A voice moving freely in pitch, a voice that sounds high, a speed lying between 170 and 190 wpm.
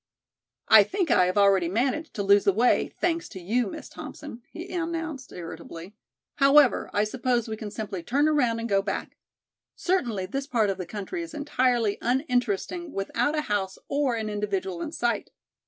Yes: wide, 6.4 semitones; high, 235 Hz; average, 175 wpm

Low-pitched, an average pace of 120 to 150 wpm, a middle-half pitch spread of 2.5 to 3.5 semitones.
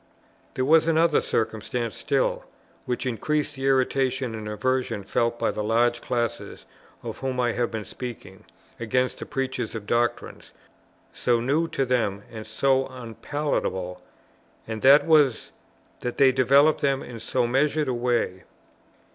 Yes: low, 125 Hz; average, 145 wpm; average, 2.8 semitones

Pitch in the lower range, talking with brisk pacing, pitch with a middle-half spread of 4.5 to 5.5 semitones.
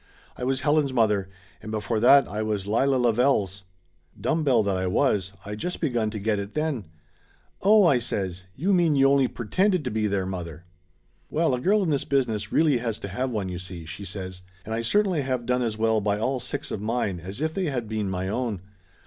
Yes: low, 115 Hz; fast, 220 wpm; average, 5.2 semitones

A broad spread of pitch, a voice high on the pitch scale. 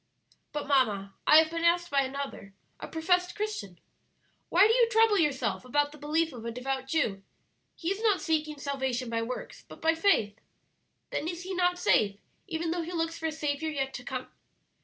No: average, 4.7 semitones; very high, 305 Hz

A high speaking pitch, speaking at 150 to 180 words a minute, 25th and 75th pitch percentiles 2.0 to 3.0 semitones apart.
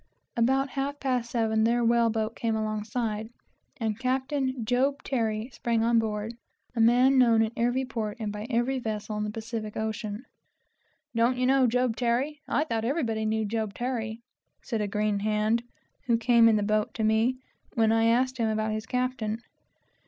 Yes: high, 230 Hz; average, 175 wpm; narrow, 2.5 semitones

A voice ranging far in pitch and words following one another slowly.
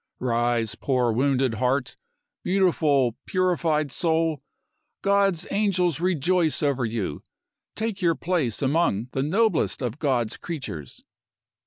Yes: wide, 6.3 semitones; slow, 110 wpm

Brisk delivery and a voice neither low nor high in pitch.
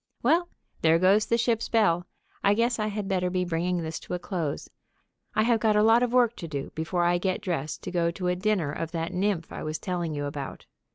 Yes: fast, 235 wpm; medium, 180 Hz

